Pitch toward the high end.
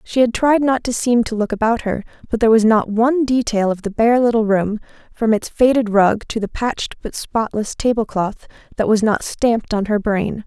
Yes: high, 225 Hz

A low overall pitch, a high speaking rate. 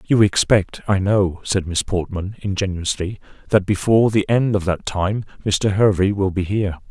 No: low, 100 Hz; average, 175 wpm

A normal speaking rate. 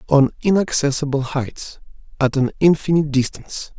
No: slow, 95 wpm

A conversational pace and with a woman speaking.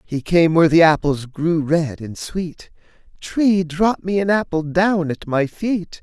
No: average, 180 wpm; male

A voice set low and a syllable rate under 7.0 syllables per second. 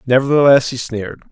Yes: low, 125 Hz; 6.3 syllables/s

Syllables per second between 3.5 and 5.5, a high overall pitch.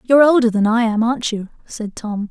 No: 5.8 syllables/s; high, 230 Hz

